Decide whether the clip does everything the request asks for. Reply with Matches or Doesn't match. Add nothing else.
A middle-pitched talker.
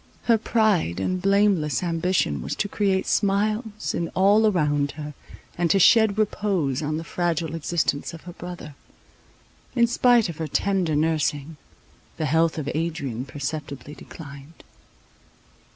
Matches